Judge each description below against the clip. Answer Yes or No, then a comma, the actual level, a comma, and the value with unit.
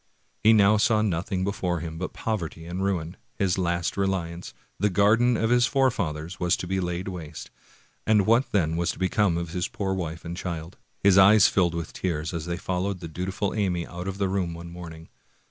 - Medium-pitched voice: No, very low, 90 Hz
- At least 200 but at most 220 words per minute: Yes, fast, 205 wpm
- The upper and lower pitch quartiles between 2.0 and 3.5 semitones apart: Yes, average, 2.8 semitones